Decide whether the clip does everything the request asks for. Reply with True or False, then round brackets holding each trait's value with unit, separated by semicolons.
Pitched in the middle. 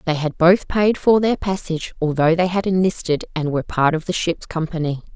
True (170 Hz)